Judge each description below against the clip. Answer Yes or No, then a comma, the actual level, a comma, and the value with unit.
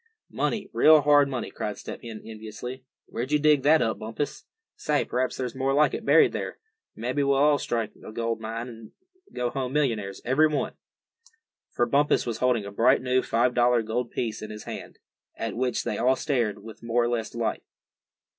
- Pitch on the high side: No, low, 125 Hz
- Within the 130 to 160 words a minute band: No, average, 190 wpm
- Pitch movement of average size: Yes, average, 3.5 semitones